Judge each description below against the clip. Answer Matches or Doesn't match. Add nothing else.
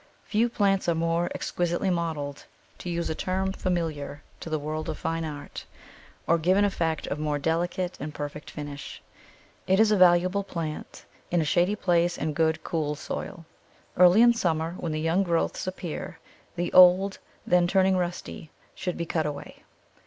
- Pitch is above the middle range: Doesn't match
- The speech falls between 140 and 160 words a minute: Doesn't match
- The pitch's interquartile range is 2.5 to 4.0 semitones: Matches